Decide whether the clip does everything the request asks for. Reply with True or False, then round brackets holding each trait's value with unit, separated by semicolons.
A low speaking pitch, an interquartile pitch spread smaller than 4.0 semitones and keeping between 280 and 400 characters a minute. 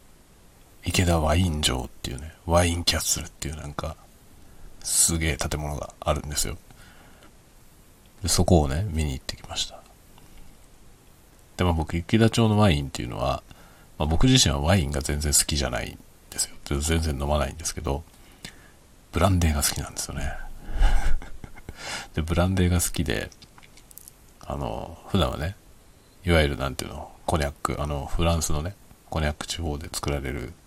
True (80 Hz; 3.5 semitones; 330 characters per minute)